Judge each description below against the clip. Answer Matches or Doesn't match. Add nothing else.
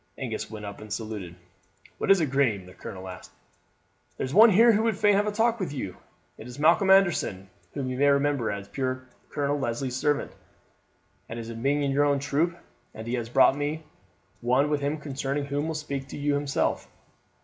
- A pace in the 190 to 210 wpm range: Matches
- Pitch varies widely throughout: Doesn't match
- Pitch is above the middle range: Doesn't match